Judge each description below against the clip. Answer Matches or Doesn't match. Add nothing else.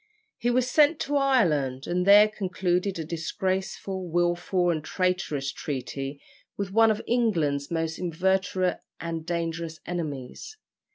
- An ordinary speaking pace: Doesn't match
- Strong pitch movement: Doesn't match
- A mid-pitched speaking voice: Matches